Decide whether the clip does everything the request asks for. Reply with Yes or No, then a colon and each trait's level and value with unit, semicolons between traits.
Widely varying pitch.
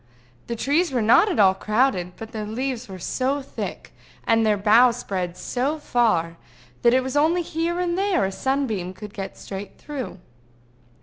Yes: wide, 5.7 semitones